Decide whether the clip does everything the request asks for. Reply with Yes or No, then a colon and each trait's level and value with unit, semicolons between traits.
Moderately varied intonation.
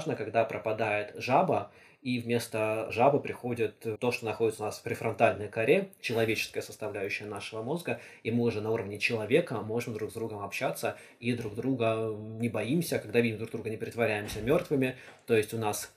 No: narrow, 1.7 semitones